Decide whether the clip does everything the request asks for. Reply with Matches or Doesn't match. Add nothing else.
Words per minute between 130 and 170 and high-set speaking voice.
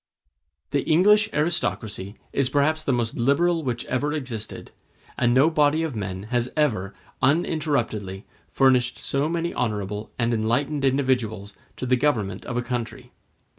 Doesn't match